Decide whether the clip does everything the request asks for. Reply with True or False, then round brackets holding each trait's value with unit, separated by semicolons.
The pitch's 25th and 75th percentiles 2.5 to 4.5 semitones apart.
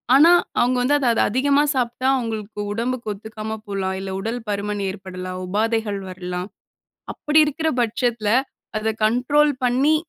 True (4.0 semitones)